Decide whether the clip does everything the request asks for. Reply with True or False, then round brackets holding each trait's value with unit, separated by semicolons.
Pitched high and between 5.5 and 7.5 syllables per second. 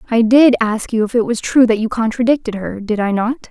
True (230 Hz; 5.6 syllables/s)